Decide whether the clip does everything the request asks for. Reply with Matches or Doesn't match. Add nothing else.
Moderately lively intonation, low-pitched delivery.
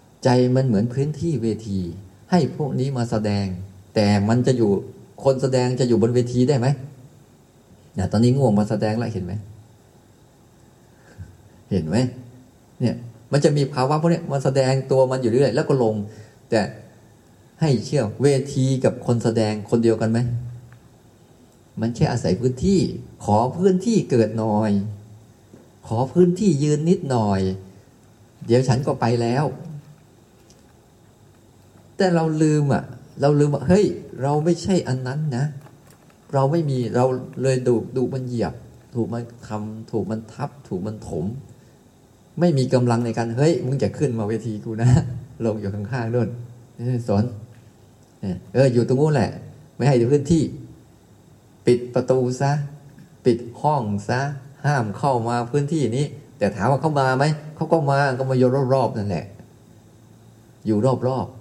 Matches